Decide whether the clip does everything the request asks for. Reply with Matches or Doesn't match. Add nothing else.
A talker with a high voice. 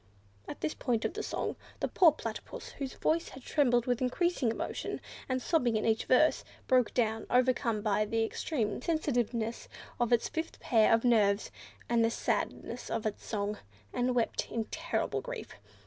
Matches